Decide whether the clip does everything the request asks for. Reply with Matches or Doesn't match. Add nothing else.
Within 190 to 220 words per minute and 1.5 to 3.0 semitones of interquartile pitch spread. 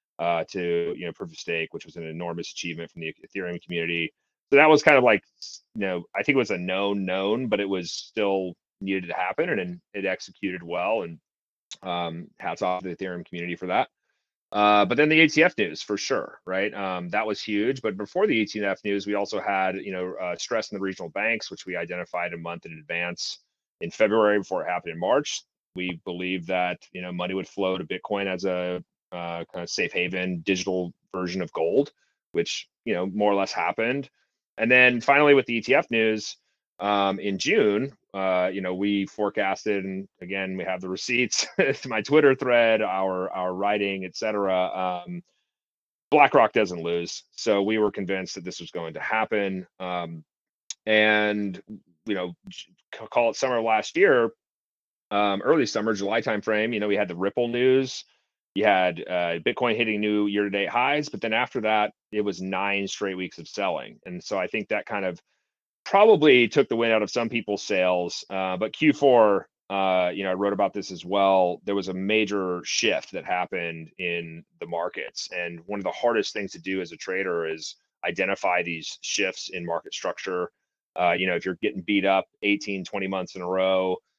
Matches